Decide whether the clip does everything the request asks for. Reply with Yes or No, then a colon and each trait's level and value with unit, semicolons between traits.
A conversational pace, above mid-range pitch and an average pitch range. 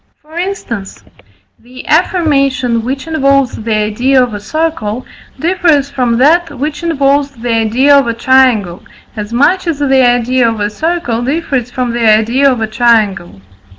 Yes: average, 155 wpm; very high, 255 Hz; average, 4.0 semitones